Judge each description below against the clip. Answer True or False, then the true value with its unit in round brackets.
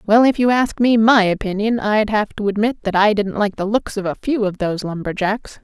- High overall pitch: True (210 Hz)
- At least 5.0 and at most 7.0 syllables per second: True (5.5 syllables/s)